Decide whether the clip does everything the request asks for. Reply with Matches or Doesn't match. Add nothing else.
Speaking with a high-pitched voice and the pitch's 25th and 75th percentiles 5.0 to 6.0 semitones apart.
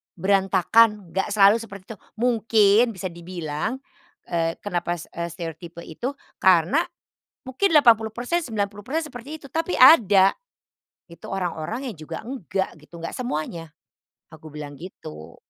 Matches